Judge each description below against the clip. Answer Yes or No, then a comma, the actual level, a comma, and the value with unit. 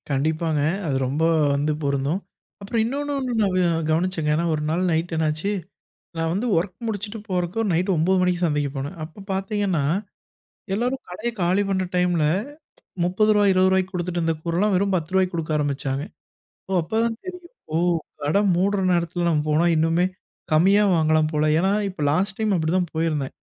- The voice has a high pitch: No, medium, 175 Hz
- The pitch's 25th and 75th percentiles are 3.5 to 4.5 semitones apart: Yes, average, 3.8 semitones